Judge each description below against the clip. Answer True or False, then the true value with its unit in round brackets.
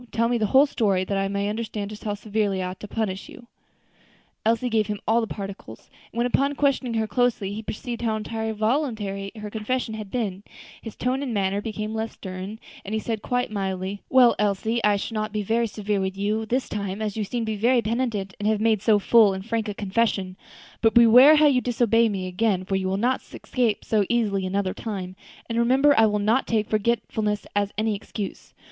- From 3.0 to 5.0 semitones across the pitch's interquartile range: False (2.5 semitones)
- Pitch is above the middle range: True (215 Hz)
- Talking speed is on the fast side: True (215 wpm)